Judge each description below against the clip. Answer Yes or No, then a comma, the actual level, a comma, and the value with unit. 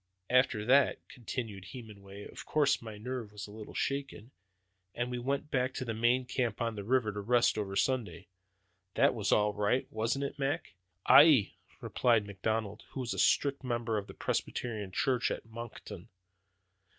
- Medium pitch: No, low, 115 Hz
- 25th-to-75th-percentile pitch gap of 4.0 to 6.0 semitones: No, average, 3.6 semitones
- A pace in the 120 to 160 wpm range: No, average, 170 wpm